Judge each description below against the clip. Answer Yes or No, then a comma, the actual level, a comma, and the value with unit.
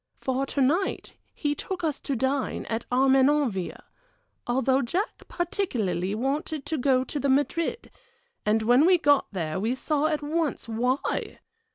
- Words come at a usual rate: Yes, average, 150 wpm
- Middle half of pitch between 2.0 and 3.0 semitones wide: No, average, 3.7 semitones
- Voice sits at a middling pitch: No, very high, 270 Hz